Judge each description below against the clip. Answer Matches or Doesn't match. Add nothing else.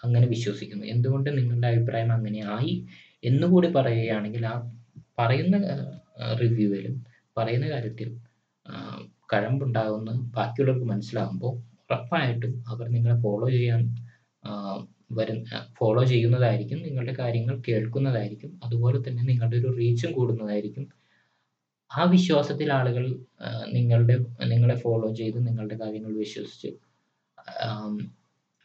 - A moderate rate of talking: Matches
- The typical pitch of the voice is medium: Doesn't match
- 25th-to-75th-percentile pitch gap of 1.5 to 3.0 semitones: Matches